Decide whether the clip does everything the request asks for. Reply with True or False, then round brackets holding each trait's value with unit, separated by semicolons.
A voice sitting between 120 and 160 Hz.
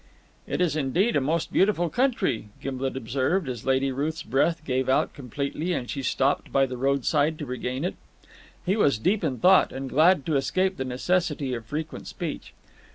True (140 Hz)